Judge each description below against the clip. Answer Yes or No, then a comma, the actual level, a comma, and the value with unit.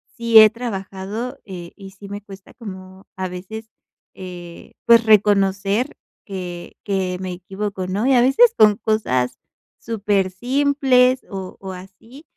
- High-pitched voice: Yes, high, 200 Hz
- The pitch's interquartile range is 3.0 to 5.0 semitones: Yes, average, 3.5 semitones